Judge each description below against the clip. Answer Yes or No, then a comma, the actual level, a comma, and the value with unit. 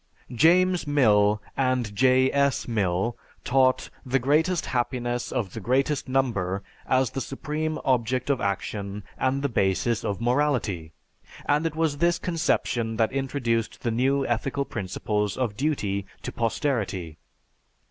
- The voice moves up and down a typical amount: Yes, average, 4.7 semitones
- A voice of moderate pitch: No, low, 125 Hz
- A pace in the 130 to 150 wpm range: Yes, slow, 135 wpm